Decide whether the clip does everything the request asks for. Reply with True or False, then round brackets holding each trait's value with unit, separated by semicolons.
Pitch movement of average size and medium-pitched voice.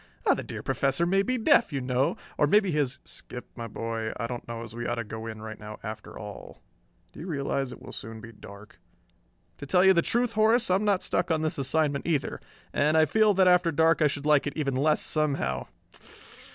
False (6.7 semitones; 145 Hz)